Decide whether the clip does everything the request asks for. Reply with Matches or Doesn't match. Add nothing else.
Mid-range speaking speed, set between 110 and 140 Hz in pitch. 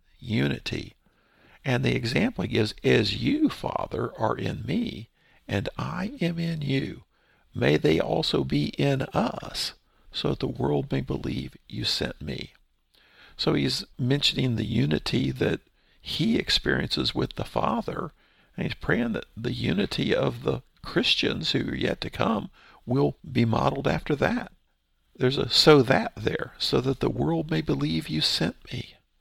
Matches